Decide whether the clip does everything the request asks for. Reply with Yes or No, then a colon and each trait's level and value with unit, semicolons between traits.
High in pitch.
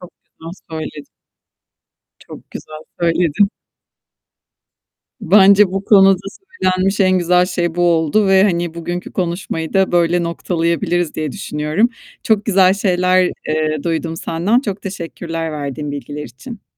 No: medium, 175 Hz